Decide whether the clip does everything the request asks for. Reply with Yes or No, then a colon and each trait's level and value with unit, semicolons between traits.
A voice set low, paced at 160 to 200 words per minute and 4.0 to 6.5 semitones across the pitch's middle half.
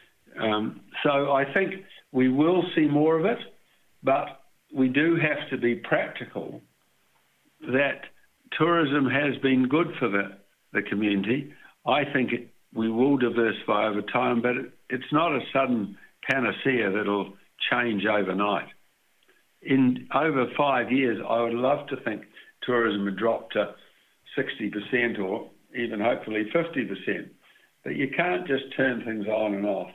No: low, 120 Hz; average, 140 wpm; average, 5.1 semitones